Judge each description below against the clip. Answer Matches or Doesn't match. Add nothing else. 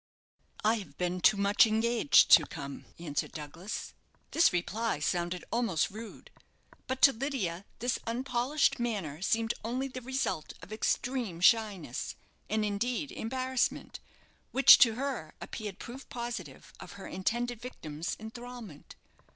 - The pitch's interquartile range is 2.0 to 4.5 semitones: Doesn't match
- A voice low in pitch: Doesn't match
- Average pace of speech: Doesn't match